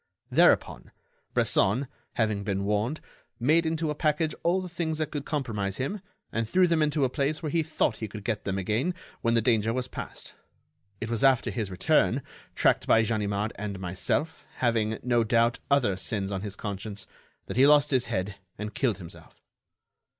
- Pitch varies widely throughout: Yes, wide, 6.2 semitones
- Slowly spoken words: No, average, 180 wpm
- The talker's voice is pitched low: Yes, low, 115 Hz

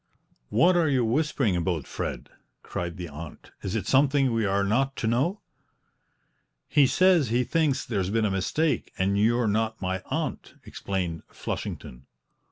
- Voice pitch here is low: Yes, low, 110 Hz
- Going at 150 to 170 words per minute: Yes, average, 155 wpm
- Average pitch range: No, wide, 6.2 semitones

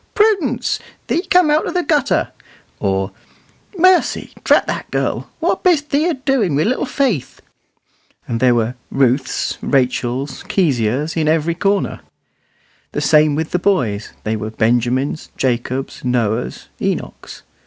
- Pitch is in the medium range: Yes, medium, 150 Hz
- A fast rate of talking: No, slow, 135 wpm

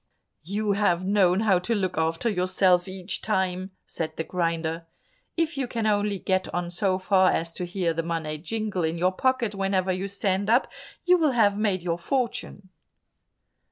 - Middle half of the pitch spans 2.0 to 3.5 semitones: Yes, average, 2.9 semitones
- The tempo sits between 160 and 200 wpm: Yes, average, 175 wpm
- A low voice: No, high, 190 Hz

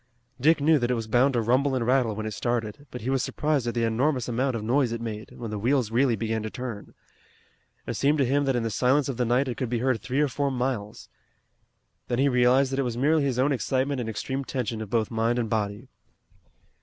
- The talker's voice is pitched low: Yes, low, 125 Hz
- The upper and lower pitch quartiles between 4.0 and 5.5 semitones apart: No, average, 3.0 semitones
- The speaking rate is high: Yes, fast, 245 wpm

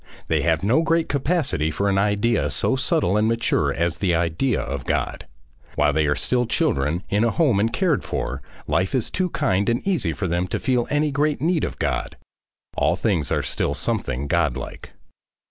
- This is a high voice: No, low, 110 Hz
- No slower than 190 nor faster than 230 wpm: Yes, average, 195 wpm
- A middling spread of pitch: No, wide, 8.6 semitones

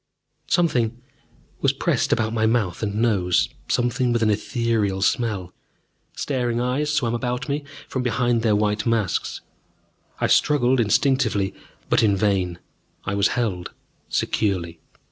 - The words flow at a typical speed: No, slow, 130 wpm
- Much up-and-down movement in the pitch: No, average, 3.3 semitones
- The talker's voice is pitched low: Yes, low, 115 Hz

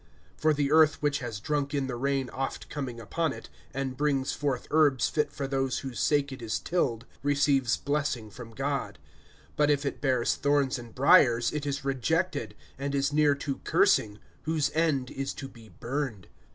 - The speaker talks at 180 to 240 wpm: Yes, average, 185 wpm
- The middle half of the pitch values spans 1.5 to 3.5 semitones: Yes, narrow, 2.4 semitones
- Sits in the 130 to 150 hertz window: Yes, medium, 140 Hz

